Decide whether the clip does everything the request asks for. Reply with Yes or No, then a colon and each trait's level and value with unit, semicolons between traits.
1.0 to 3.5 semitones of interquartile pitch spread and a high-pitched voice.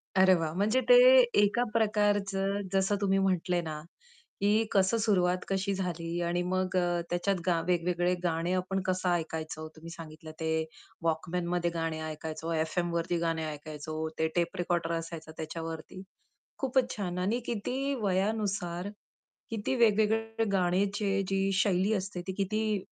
No: average, 3.2 semitones; medium, 180 Hz